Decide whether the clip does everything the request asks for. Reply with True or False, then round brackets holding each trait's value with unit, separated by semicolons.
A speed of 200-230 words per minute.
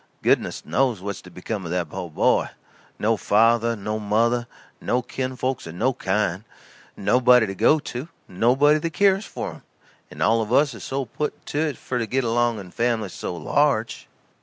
False (185 wpm)